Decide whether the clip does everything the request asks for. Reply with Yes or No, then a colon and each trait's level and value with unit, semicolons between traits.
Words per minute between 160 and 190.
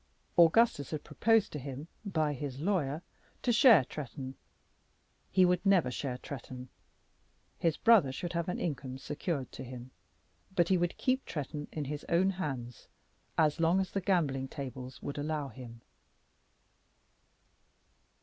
No: average, 140 wpm